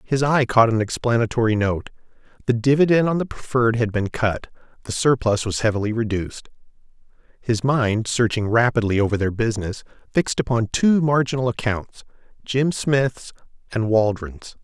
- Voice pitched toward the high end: No, low, 120 Hz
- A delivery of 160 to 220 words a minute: No, average, 140 wpm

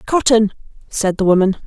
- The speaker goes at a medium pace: Yes, average, 145 wpm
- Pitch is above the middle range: Yes, high, 210 Hz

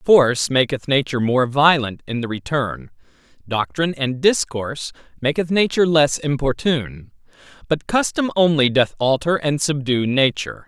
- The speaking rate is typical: No, slow, 130 wpm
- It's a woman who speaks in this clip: No, male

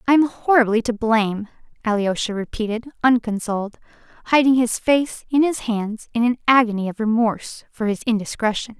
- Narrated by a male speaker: No, female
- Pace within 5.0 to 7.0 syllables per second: Yes, 5.4 syllables/s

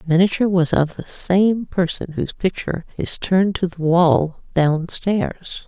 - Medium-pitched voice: Yes, medium, 175 Hz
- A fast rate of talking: No, average, 170 wpm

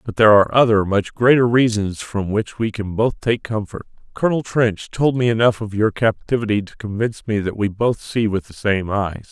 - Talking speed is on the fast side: Yes, fast, 215 wpm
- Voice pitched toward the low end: Yes, low, 110 Hz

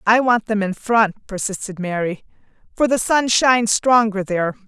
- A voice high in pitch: Yes, high, 215 Hz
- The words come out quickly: No, average, 165 wpm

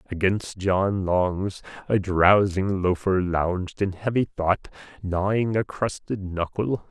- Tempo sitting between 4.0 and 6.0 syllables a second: No, 3.6 syllables/s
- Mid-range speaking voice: No, very low, 95 Hz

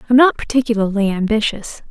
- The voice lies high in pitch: Yes, high, 225 Hz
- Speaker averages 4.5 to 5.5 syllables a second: No, 6.1 syllables/s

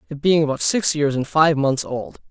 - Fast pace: Yes, fast, 235 wpm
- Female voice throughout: No, male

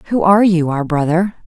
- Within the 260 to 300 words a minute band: No, average, 200 wpm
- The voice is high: No, medium, 175 Hz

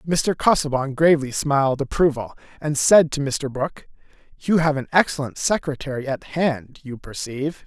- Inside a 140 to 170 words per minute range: Yes, average, 150 wpm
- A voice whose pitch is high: No, medium, 145 Hz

